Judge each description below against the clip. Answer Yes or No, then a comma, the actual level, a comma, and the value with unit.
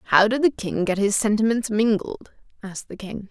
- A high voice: Yes, high, 210 Hz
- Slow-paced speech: No, average, 200 wpm